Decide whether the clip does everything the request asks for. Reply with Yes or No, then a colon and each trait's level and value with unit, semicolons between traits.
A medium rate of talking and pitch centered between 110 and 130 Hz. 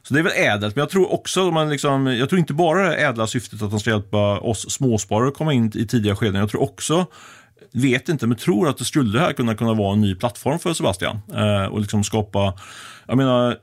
No: fast, 240 wpm; low, 120 Hz